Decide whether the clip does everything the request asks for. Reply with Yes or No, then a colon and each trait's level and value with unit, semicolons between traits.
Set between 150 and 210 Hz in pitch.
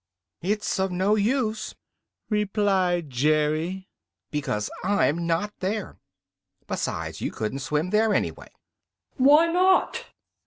Yes: high, 190 Hz